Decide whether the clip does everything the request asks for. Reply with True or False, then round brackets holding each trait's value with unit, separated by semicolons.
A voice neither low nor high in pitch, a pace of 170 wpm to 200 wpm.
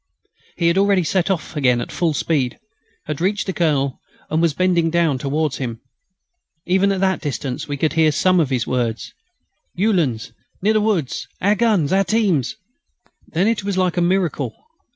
True (170 Hz; 175 wpm)